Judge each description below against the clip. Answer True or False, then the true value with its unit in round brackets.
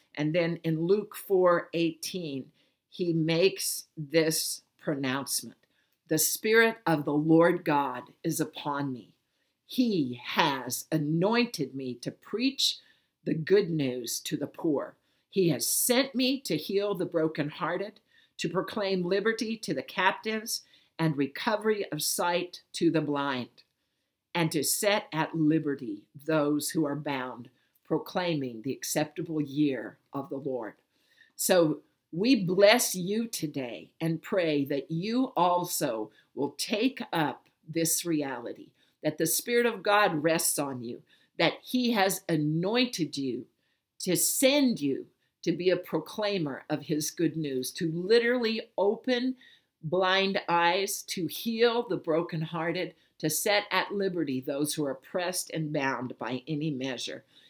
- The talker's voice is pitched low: False (165 Hz)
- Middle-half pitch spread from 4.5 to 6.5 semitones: True (4.8 semitones)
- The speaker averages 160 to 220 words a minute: False (135 wpm)